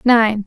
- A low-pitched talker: No, high, 225 Hz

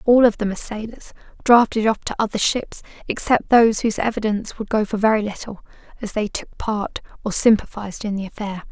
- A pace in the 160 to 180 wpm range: No, average, 195 wpm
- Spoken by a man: No, female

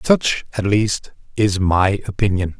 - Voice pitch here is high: No, low, 100 Hz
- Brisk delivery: No, average, 140 wpm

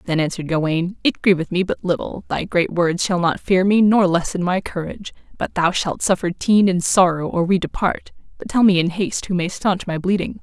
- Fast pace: Yes, fast, 225 wpm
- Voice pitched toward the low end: No, medium, 180 Hz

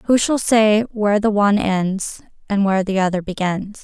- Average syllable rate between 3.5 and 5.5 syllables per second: Yes, 4.9 syllables/s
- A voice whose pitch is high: Yes, high, 205 Hz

